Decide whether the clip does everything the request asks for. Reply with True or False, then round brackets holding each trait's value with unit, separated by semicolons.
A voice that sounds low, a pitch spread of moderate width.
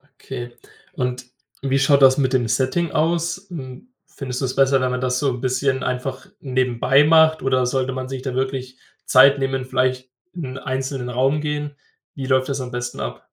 False (130 Hz; 1.6 semitones)